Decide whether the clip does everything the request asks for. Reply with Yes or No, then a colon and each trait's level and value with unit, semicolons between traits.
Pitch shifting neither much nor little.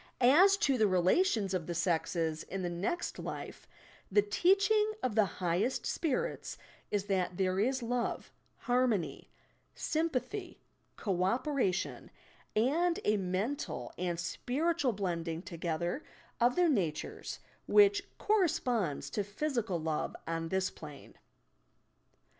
No: wide, 8.6 semitones